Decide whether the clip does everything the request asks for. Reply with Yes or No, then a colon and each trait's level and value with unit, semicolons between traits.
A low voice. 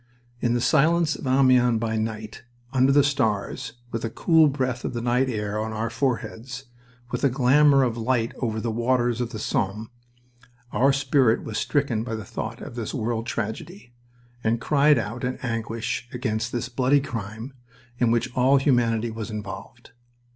Yes: low, 120 Hz